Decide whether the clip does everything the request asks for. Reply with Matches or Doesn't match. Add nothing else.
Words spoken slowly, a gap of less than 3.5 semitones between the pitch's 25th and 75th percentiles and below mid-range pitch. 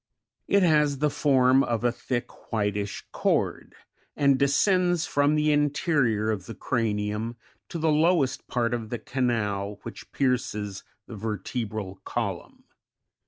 Doesn't match